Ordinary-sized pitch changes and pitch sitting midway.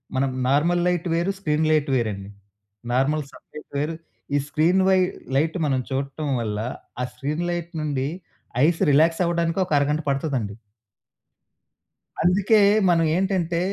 Yes: average, 3.8 semitones; medium, 155 Hz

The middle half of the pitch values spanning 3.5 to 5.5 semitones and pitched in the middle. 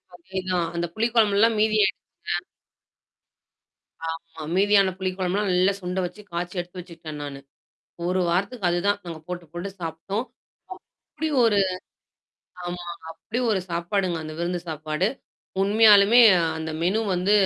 No: average, 2.8 semitones; medium, 180 Hz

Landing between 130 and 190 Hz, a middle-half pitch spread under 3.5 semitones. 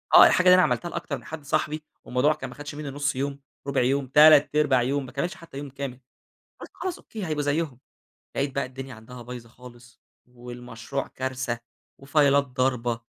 Yes: low, 135 Hz; average, 2.9 semitones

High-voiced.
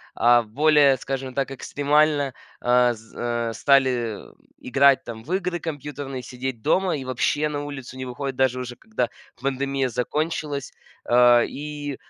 No: low, 135 Hz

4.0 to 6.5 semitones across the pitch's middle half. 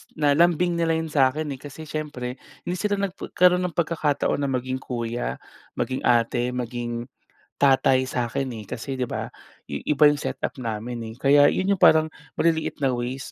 Yes: average, 4.3 semitones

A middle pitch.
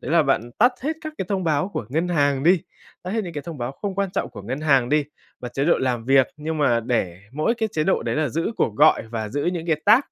Yes: medium, 150 Hz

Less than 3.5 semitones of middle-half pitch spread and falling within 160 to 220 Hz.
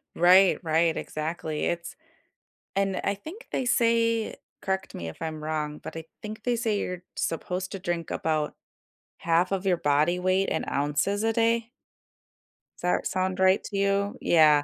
No: average, 3.9 semitones; medium, 185 Hz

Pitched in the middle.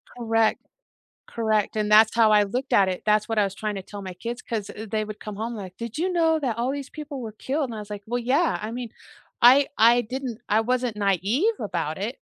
No: high, 225 Hz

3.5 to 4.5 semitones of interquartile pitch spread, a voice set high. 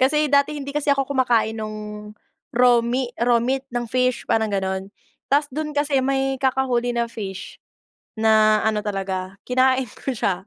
Yes: average, 3.9 semitones; high, 240 Hz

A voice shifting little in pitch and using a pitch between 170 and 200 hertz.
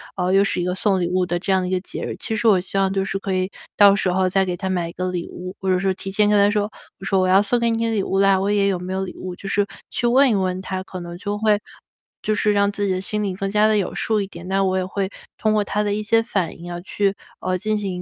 Yes: narrow, 2.0 semitones; high, 195 Hz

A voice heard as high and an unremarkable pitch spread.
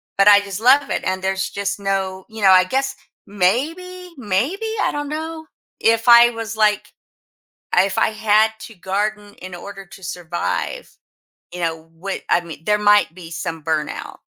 Yes: high, 205 Hz; average, 4.0 semitones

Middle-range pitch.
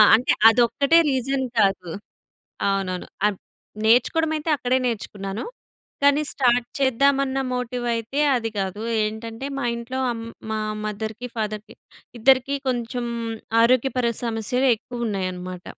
No: high, 235 Hz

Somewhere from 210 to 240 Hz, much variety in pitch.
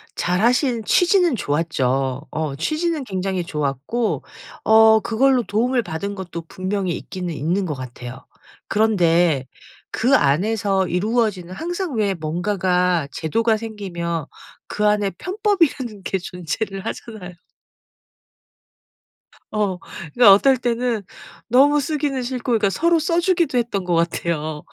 No: high, 200 Hz; wide, 6.2 semitones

